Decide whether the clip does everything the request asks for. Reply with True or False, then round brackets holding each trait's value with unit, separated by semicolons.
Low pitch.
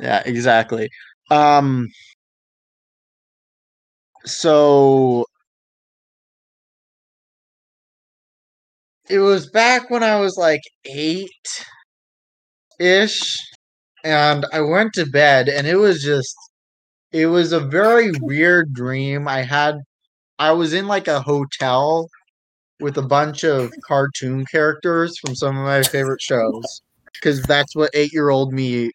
False (150 Hz)